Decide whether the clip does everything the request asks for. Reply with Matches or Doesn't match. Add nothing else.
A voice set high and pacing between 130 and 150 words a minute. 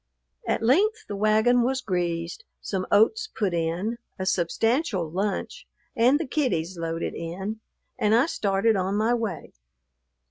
Matches